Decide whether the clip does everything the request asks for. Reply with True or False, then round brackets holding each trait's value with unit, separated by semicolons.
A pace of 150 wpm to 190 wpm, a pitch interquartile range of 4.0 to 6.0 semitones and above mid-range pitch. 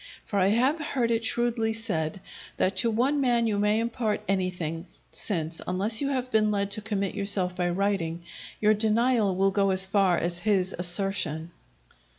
False (170 wpm; 3.5 semitones; 200 Hz)